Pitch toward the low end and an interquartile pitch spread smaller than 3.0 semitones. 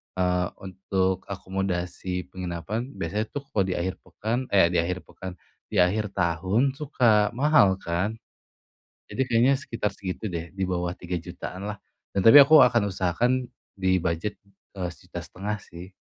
No: very low, 95 Hz; average, 3.3 semitones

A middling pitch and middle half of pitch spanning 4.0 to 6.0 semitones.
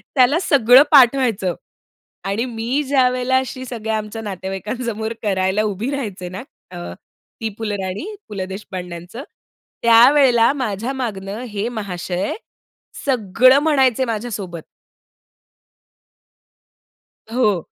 No: high, 225 Hz; average, 4.6 semitones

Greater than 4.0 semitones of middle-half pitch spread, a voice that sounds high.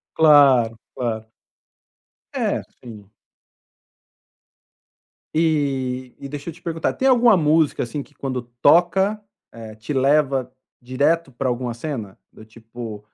No: average, 4.7 semitones; low, 135 Hz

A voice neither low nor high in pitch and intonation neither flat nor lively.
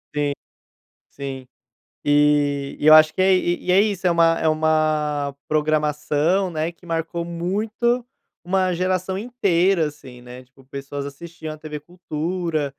Yes: medium, 155 Hz; average, 3.6 semitones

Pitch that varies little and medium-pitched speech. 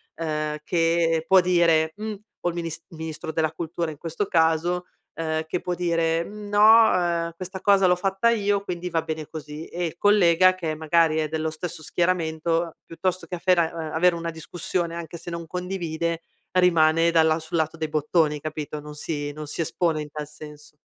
Yes: narrow, 2.1 semitones; medium, 165 Hz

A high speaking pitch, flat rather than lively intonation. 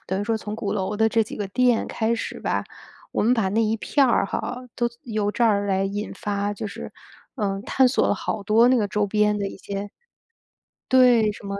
Yes: high, 210 Hz; narrow, 2.2 semitones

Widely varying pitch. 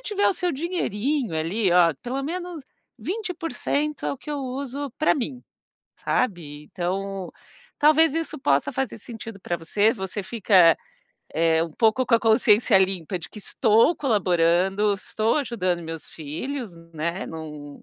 Yes: wide, 7.8 semitones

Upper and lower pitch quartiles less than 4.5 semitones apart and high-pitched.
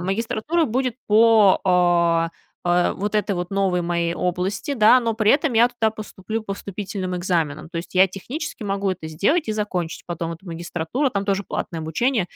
Yes: average, 4.1 semitones; high, 195 Hz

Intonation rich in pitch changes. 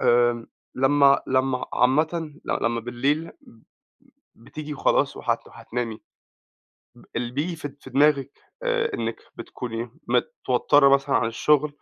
No: average, 3.9 semitones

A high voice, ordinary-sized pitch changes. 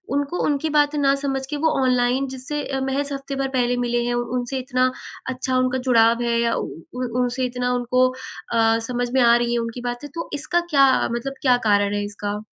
No: very high, 250 Hz; narrow, 2.3 semitones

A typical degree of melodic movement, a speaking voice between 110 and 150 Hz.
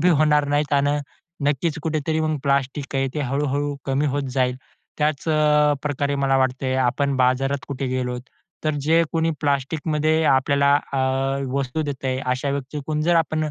No: narrow, 2.1 semitones; medium, 140 Hz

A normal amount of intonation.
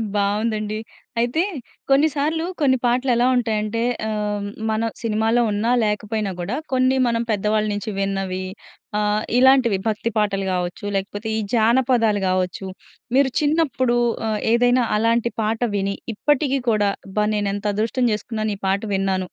Yes: average, 3.1 semitones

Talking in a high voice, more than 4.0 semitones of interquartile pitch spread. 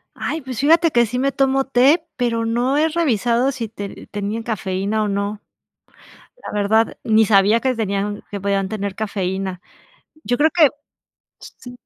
Yes: high, 225 Hz; average, 4.5 semitones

